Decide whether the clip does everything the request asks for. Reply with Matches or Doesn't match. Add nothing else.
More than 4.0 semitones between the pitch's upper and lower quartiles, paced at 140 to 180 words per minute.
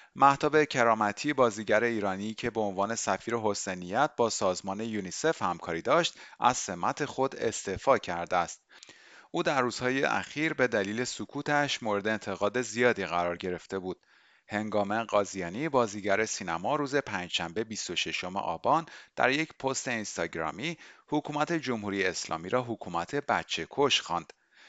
Doesn't match